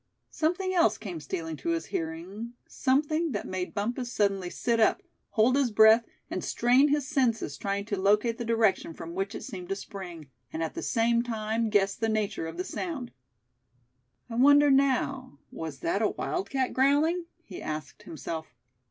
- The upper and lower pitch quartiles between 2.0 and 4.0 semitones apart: No, wide, 5.6 semitones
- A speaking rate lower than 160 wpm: No, average, 170 wpm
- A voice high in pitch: Yes, high, 220 Hz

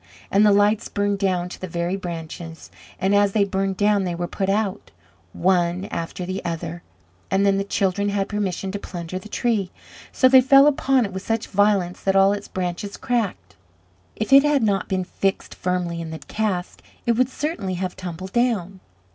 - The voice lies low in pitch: No, high, 195 Hz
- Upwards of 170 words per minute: Yes, average, 190 wpm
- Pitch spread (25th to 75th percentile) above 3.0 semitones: No, narrow, 2.6 semitones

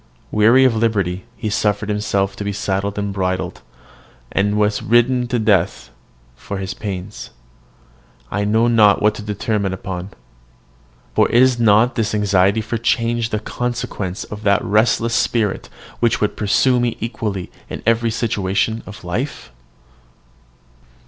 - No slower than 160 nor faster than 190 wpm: No, average, 140 wpm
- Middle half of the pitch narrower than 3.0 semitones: Yes, narrow, 2.6 semitones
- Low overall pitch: Yes, low, 105 Hz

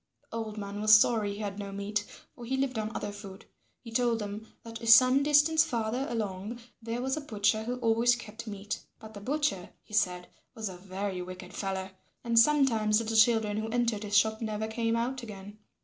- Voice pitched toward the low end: No, high, 220 Hz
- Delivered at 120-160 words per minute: No, average, 200 wpm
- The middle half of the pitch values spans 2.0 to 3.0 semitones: Yes, narrow, 2.5 semitones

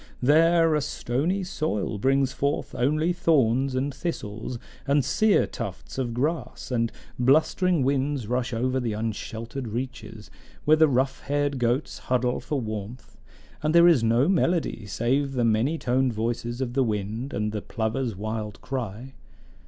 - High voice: No, low, 130 Hz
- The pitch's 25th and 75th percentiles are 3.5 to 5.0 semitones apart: Yes, average, 4.1 semitones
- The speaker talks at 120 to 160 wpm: Yes, average, 150 wpm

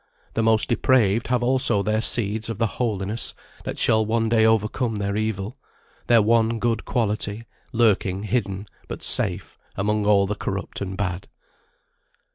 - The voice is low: Yes, low, 110 Hz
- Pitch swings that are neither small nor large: No, narrow, 2.2 semitones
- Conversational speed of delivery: Yes, average, 150 wpm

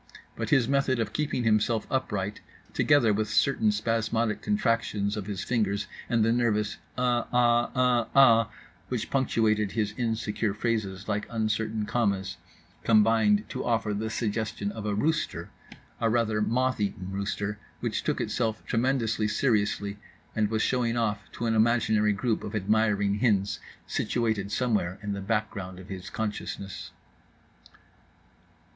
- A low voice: Yes, low, 110 Hz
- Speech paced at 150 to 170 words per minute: No, average, 140 wpm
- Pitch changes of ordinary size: No, narrow, 2.3 semitones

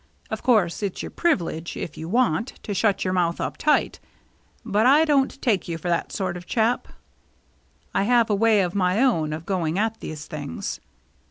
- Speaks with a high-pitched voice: Yes, high, 195 Hz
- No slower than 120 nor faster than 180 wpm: No, average, 195 wpm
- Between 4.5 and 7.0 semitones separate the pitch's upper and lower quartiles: Yes, average, 5.1 semitones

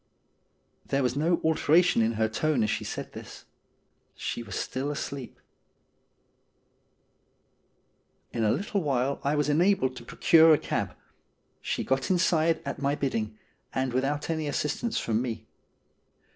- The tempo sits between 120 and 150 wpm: Yes, average, 145 wpm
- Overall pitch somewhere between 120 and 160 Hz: Yes, medium, 140 Hz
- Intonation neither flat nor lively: Yes, average, 4.4 semitones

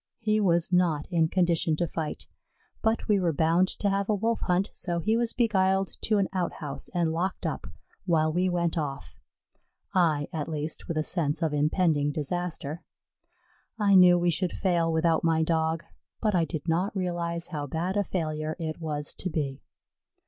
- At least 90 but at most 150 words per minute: No, average, 180 wpm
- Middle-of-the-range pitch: Yes, medium, 170 Hz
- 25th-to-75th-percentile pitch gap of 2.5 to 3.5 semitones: Yes, average, 2.9 semitones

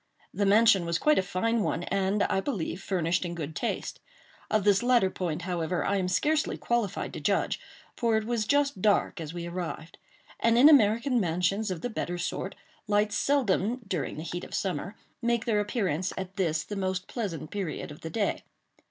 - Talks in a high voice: Yes, high, 195 Hz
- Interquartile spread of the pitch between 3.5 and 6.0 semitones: Yes, average, 4.2 semitones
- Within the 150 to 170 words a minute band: No, average, 190 wpm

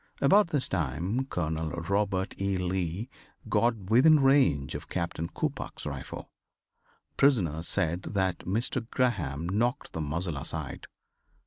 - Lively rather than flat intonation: Yes, wide, 6.9 semitones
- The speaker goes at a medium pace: No, slow, 120 wpm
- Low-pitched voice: Yes, very low, 95 Hz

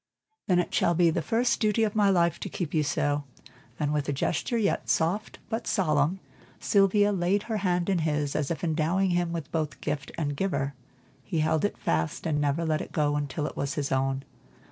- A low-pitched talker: No, medium, 165 Hz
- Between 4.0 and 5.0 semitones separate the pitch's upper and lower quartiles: Yes, average, 4.5 semitones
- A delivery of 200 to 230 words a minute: Yes, fast, 205 wpm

